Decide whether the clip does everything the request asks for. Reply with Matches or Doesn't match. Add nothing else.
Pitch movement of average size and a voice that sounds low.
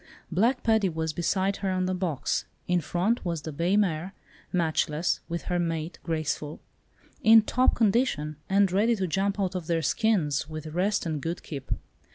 Doesn't match